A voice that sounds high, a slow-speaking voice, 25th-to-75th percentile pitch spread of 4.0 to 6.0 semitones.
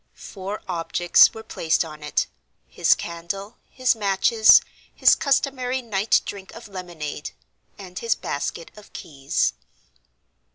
Yes: high, 195 Hz; slow, 120 wpm; average, 4.6 semitones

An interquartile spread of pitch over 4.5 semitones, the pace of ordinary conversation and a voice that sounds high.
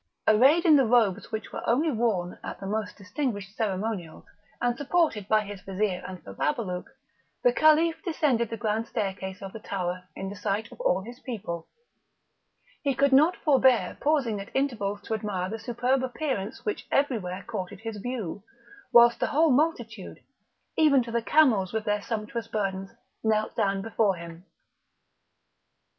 Yes: average, 4.9 semitones; average, 160 wpm; high, 220 Hz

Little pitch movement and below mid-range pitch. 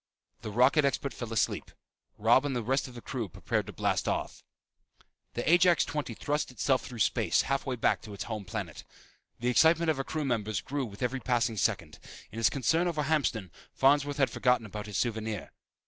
No: average, 4.3 semitones; low, 125 Hz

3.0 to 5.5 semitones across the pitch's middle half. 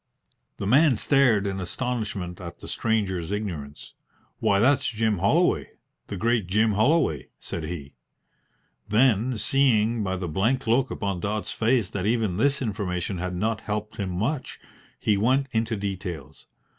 Yes: average, 4.0 semitones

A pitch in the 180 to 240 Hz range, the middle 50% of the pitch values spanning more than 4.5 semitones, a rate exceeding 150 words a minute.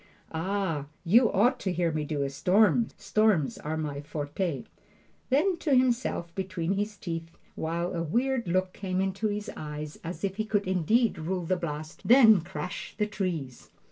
Yes: medium, 185 Hz; average, 4.9 semitones; average, 170 wpm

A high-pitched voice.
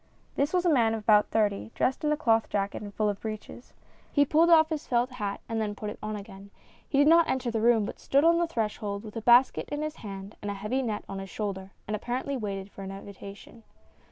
Yes: high, 220 Hz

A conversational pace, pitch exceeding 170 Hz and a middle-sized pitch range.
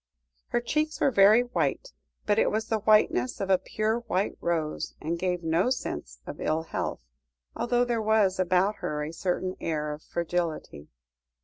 Yes: average, 175 wpm; high, 190 Hz; average, 4.9 semitones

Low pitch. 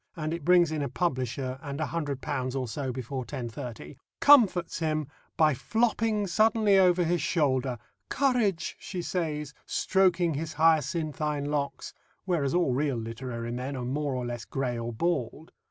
No: medium, 150 Hz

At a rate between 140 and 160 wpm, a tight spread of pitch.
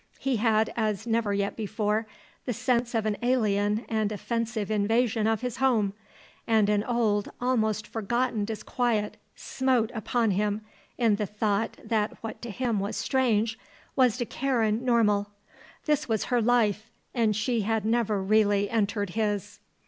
Yes: average, 150 wpm; narrow, 2.3 semitones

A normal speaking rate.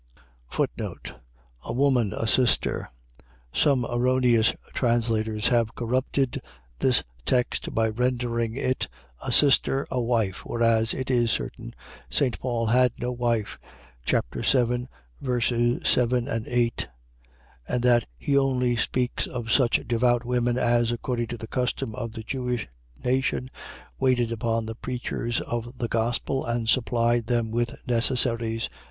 No: slow, 130 wpm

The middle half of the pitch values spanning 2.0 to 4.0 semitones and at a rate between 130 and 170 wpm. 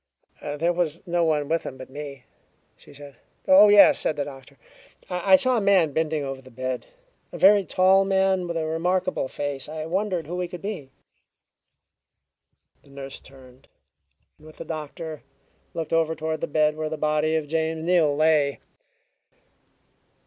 Yes: average, 3.6 semitones; average, 165 wpm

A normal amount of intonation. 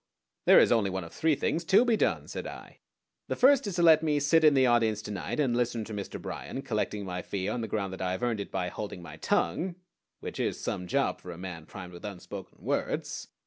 No: wide, 7.8 semitones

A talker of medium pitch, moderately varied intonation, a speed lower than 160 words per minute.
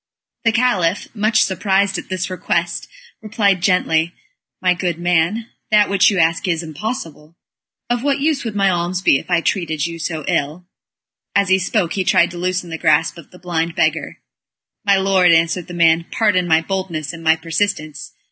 No: medium, 180 Hz; average, 3.3 semitones; average, 185 wpm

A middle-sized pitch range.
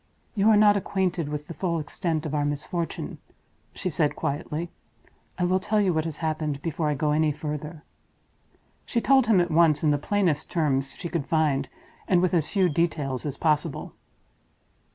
Yes: average, 3.2 semitones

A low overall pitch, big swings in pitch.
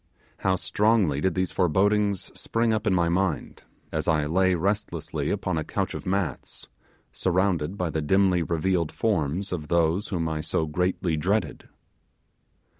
No: very low, 90 Hz; average, 3.4 semitones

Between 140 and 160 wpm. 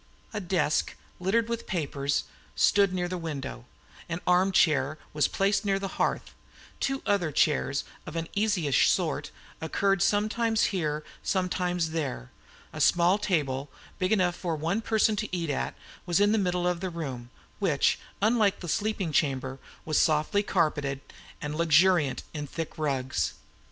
Yes: average, 150 wpm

